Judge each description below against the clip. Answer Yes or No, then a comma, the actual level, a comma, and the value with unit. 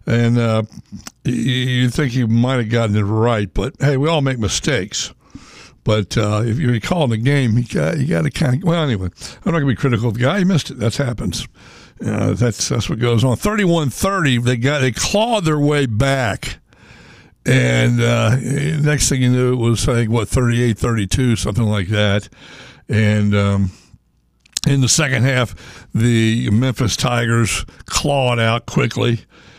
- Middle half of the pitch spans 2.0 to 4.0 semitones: Yes, average, 3.6 semitones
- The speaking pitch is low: Yes, low, 120 Hz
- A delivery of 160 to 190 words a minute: Yes, average, 180 wpm